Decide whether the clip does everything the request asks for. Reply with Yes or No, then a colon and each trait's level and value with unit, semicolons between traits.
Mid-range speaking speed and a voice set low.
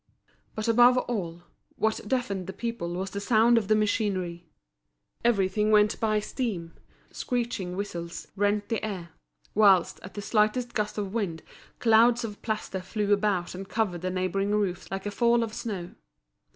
No: average, 160 wpm; high, 205 Hz